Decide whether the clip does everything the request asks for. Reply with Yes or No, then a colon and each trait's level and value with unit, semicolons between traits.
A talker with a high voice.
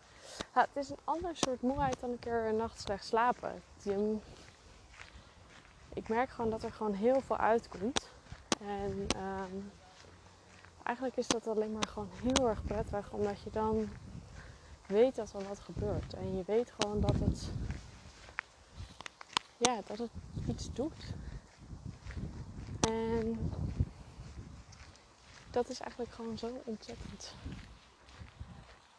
Yes: high, 220 Hz